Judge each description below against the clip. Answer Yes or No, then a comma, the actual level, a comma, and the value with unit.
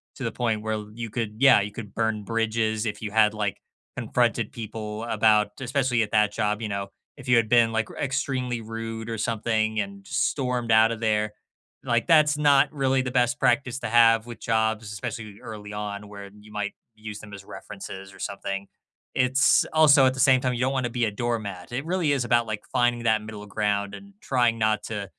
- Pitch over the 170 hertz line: No, low, 110 Hz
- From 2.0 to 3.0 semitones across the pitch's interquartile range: Yes, average, 2.7 semitones